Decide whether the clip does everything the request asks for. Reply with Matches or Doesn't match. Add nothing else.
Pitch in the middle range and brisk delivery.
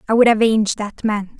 Doesn't match